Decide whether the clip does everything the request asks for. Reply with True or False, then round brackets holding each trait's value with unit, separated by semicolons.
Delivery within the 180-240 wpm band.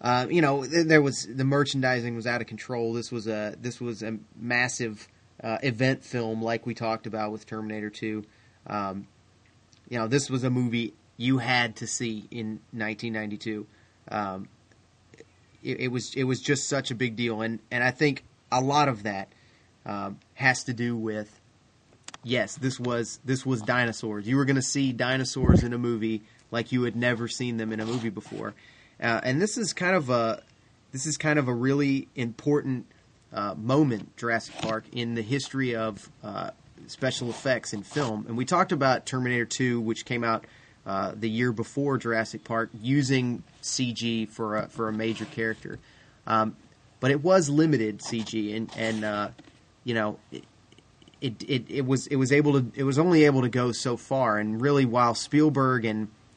True (185 wpm)